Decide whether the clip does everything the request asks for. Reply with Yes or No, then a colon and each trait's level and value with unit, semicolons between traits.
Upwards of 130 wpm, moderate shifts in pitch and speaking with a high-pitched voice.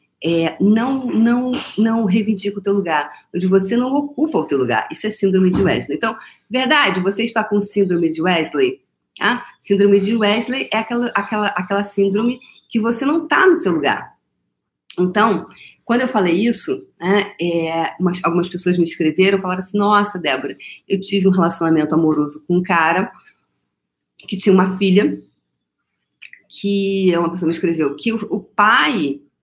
Yes: average, 165 wpm; average, 4.4 semitones; high, 200 Hz